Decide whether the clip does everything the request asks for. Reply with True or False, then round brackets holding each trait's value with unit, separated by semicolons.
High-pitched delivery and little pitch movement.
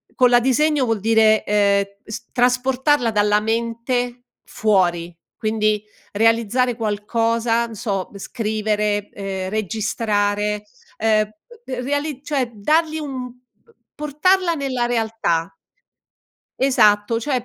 False (225 Hz; 3.2 semitones)